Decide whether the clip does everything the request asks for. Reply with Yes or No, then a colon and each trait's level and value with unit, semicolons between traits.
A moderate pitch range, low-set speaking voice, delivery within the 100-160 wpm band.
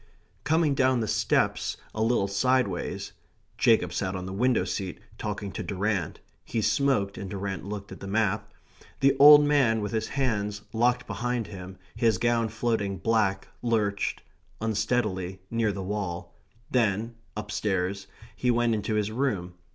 Yes: average, 3.4 semitones; low, 110 Hz; average, 150 wpm